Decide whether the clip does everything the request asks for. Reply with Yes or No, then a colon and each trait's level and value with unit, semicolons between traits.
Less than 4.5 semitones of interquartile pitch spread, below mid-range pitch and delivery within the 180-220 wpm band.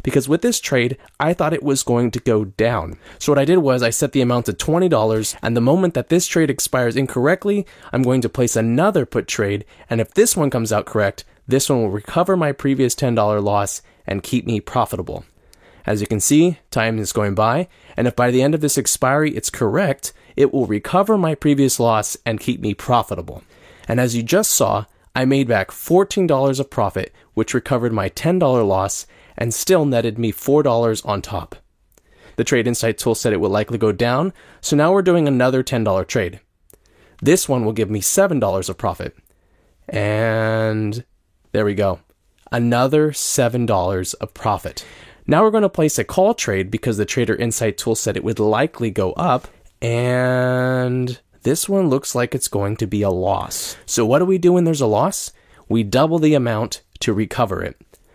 No: average, 4.9 semitones; low, 120 Hz; average, 190 wpm